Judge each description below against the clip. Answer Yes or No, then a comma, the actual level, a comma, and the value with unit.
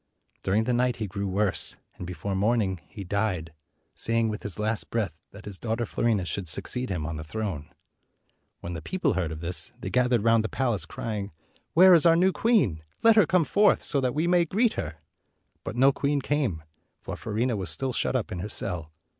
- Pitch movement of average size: No, wide, 6.0 semitones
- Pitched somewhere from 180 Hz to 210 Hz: No, low, 110 Hz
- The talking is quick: Yes, fast, 215 wpm